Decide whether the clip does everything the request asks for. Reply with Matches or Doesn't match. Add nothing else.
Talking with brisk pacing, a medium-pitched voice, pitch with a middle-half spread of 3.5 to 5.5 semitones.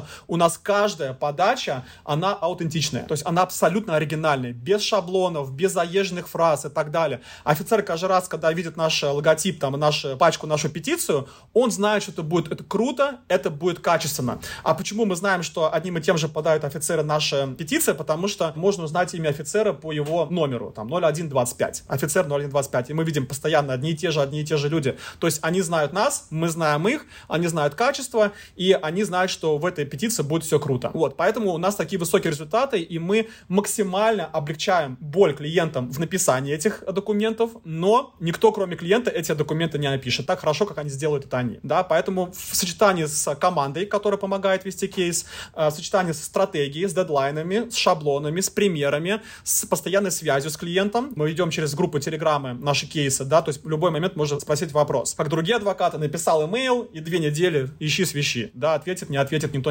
Matches